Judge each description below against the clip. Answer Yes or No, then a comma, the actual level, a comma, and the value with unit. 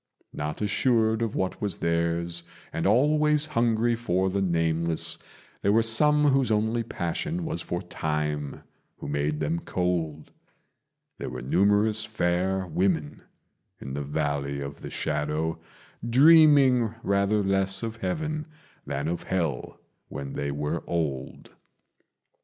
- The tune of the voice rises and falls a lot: Yes, wide, 6.4 semitones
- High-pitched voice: No, very low, 95 Hz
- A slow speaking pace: Yes, slow, 130 wpm